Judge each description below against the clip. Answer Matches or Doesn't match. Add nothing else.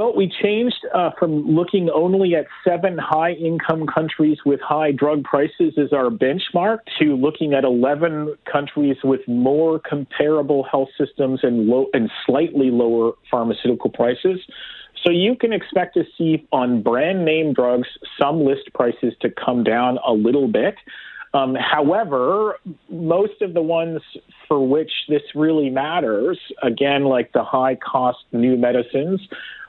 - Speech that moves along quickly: Doesn't match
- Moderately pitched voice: Matches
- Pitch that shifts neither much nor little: Matches